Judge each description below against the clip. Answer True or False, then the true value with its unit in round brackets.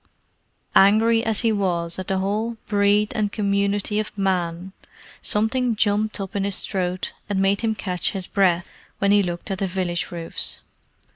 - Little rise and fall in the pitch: True (2.2 semitones)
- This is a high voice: True (200 Hz)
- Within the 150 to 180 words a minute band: True (165 wpm)